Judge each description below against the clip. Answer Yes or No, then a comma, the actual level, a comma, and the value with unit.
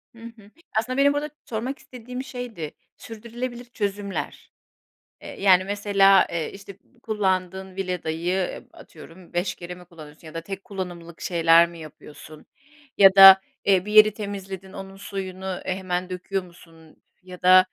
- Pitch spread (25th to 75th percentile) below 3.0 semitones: Yes, narrow, 2.6 semitones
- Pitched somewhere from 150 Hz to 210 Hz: Yes, high, 190 Hz